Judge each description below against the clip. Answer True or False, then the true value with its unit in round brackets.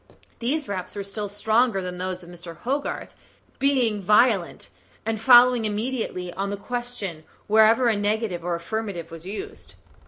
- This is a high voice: True (210 Hz)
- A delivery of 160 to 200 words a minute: False (150 wpm)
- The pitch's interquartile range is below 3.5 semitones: False (4.7 semitones)